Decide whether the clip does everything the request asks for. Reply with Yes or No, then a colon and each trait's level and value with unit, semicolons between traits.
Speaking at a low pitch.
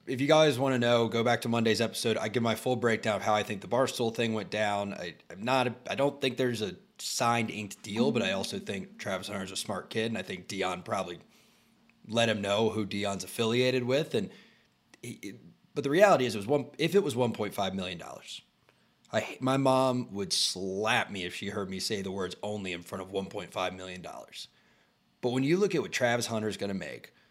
Yes: low, 115 Hz